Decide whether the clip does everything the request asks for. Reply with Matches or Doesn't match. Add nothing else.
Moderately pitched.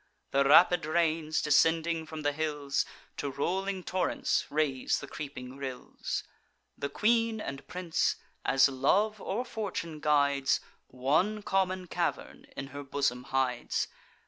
Matches